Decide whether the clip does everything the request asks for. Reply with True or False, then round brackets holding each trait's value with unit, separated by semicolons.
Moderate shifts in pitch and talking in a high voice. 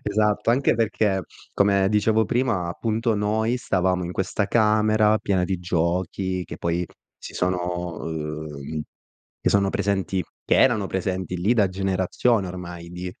False (3.2 semitones; 95 Hz)